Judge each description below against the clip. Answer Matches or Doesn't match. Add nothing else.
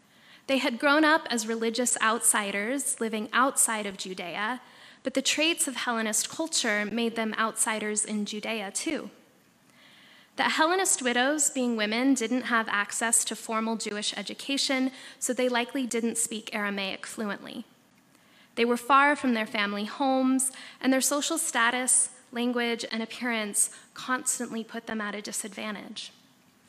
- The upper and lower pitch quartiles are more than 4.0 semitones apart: Doesn't match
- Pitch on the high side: Matches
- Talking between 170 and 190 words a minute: Doesn't match